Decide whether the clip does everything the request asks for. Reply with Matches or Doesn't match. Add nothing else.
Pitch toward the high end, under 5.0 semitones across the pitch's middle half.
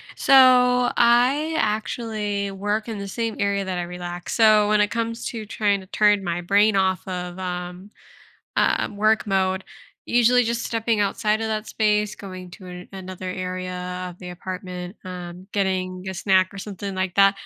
Matches